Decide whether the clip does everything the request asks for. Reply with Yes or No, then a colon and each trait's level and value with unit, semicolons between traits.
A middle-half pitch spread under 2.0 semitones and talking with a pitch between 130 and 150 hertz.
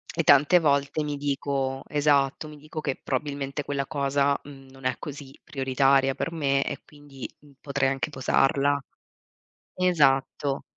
Yes: narrow, 1.3 semitones; medium, 140 Hz